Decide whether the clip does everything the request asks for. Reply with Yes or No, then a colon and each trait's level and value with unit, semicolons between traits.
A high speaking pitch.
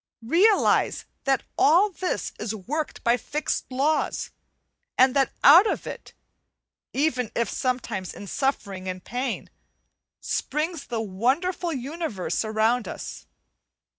Yes: very high, 260 Hz